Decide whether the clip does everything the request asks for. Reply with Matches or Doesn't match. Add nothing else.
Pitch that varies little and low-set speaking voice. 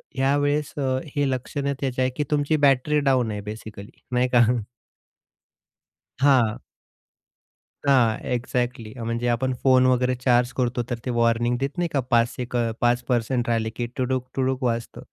Matches